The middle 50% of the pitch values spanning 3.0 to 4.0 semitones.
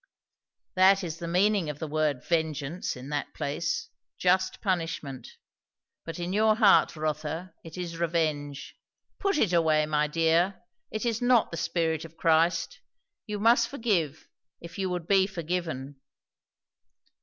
Yes: average, 3.5 semitones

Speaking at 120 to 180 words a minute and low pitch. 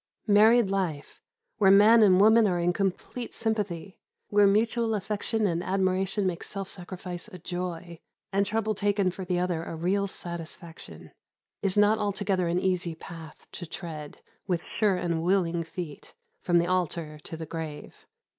No: average, 155 wpm; medium, 185 Hz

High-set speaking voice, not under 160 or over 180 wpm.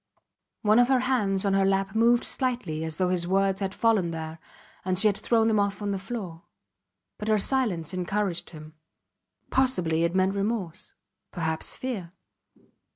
Yes: high, 195 Hz; average, 165 wpm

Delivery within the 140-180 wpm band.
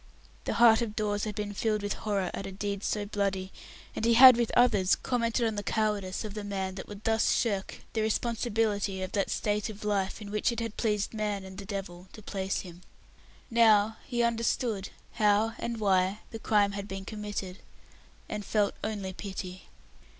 No: average, 190 wpm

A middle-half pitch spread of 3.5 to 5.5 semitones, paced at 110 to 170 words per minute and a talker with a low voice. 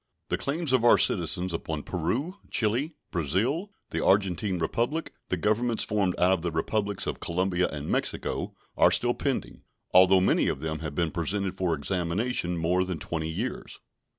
Yes: average, 4.6 semitones; average, 165 wpm; very low, 95 Hz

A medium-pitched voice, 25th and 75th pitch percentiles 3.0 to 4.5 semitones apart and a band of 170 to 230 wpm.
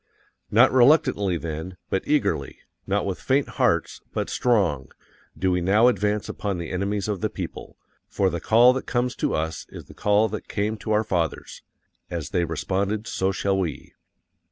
No: low, 100 Hz; average, 3.6 semitones; average, 175 wpm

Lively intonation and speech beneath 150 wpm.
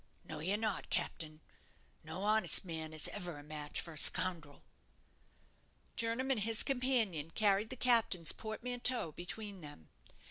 Yes: wide, 6.0 semitones; average, 140 wpm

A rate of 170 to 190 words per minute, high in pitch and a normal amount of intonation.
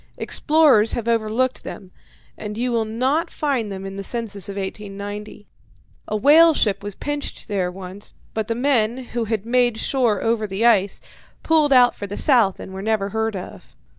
Yes: average, 180 wpm; high, 220 Hz; average, 3.5 semitones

